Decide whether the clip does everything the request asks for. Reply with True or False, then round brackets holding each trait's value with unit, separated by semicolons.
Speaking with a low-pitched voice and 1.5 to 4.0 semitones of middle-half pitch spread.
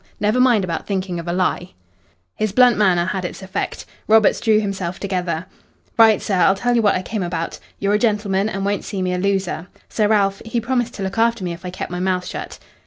False (195 Hz; 2.9 semitones)